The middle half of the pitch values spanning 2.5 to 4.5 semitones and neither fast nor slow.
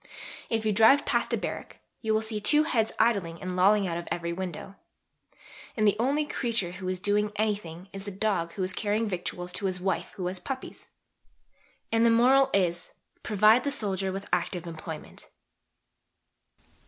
Yes: average, 3.5 semitones; average, 175 wpm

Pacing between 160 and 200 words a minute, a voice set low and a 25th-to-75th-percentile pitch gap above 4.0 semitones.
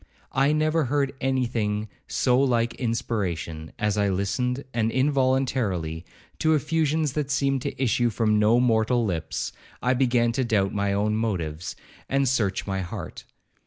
No: average, 150 wpm; low, 120 Hz; average, 4.5 semitones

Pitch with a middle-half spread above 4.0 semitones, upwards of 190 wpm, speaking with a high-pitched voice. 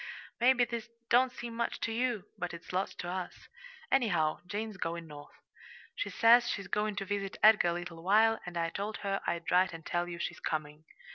Yes: average, 4.7 semitones; average, 200 wpm; high, 195 Hz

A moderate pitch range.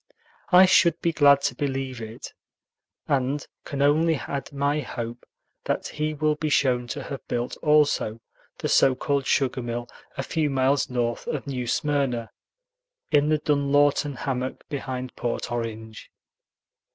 Yes: average, 3.0 semitones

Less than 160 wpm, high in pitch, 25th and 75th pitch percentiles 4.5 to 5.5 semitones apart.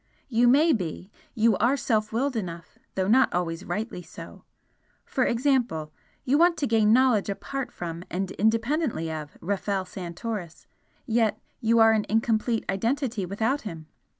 Yes: average, 150 wpm; high, 220 Hz; average, 4.8 semitones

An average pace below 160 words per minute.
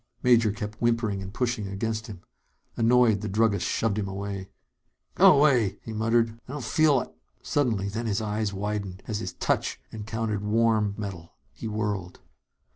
No: average, 165 wpm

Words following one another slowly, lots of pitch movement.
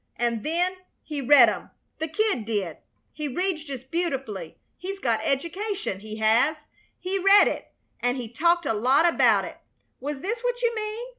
No: average, 170 wpm; wide, 7.8 semitones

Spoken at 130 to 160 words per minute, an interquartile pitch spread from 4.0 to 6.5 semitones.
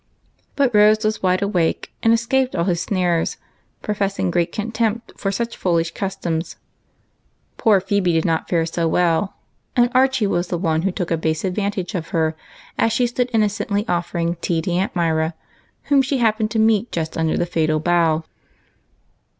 No: average, 170 wpm; average, 4.4 semitones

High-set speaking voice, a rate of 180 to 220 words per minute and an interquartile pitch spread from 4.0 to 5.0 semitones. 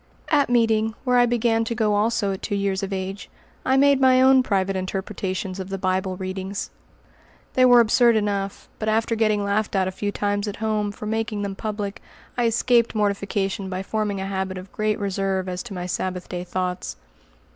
No: high, 205 Hz; average, 195 wpm; average, 2.7 semitones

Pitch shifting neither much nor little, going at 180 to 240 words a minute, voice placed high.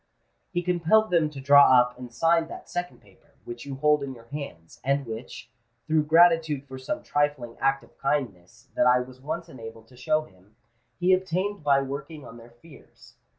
No: average, 4.6 semitones; average, 190 wpm; medium, 140 Hz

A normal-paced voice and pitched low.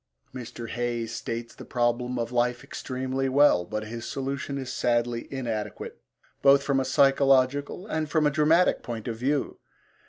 Yes: average, 155 wpm; low, 130 Hz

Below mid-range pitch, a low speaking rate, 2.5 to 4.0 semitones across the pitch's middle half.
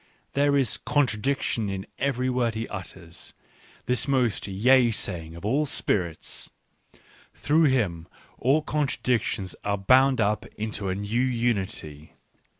No: low, 115 Hz; slow, 130 wpm; average, 5.2 semitones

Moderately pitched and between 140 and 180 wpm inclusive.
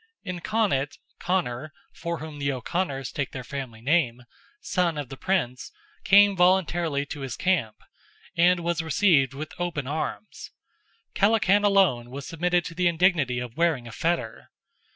Yes: medium, 160 Hz; average, 150 wpm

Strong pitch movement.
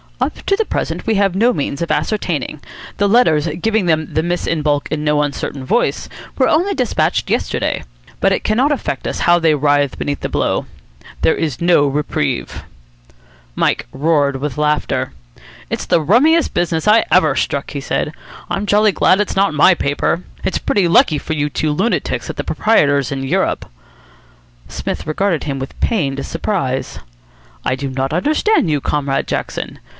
Yes: wide, 6.0 semitones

